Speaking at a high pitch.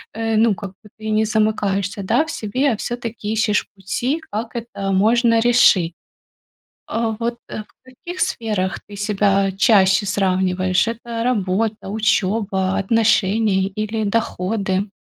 Yes: high, 215 Hz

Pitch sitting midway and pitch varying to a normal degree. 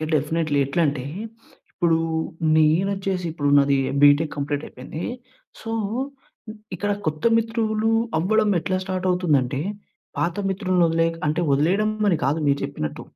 Yes: medium, 165 Hz; average, 4.7 semitones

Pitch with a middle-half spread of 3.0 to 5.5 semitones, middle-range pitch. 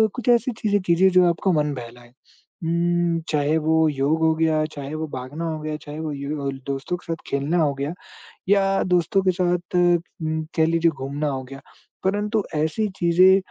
Yes: average, 3.4 semitones; medium, 160 Hz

